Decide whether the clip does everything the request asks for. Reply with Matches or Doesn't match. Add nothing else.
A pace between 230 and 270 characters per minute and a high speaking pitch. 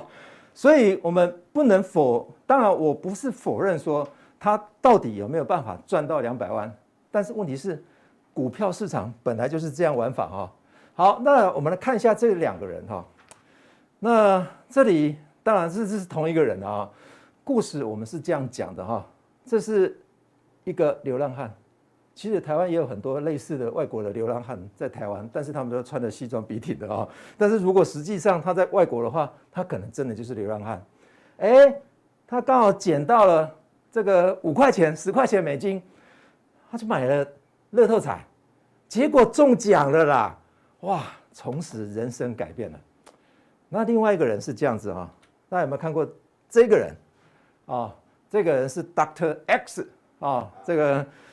Doesn't match